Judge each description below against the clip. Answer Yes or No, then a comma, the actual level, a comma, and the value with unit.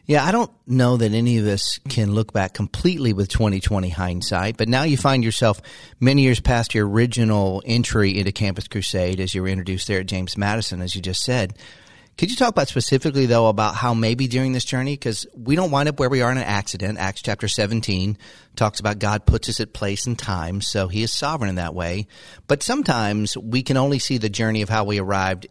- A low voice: Yes, low, 110 Hz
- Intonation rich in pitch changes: No, average, 4.1 semitones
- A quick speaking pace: Yes, fast, 225 wpm